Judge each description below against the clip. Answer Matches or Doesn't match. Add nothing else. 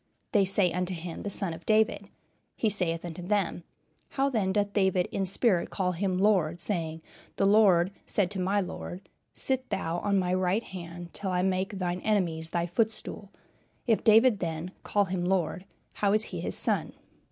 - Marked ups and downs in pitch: Doesn't match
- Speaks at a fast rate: Doesn't match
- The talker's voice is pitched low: Doesn't match